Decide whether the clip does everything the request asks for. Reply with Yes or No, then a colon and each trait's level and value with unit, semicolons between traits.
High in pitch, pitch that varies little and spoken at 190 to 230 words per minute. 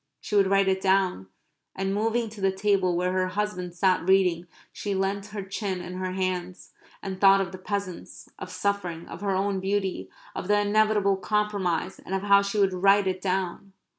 Yes: high, 195 Hz; narrow, 1.6 semitones; average, 195 wpm